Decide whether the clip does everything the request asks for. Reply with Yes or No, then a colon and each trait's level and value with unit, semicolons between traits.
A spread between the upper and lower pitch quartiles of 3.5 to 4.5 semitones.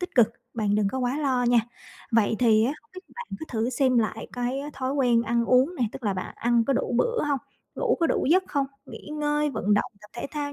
Yes: average, 4.2 semitones